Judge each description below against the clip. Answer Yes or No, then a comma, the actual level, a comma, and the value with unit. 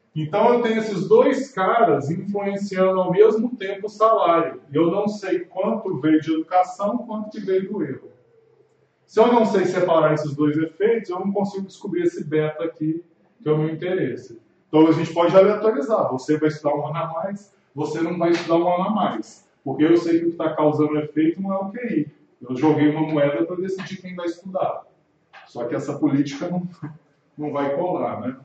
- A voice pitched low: No, medium, 175 Hz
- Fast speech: Yes, fast, 200 wpm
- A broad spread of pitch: No, average, 4.3 semitones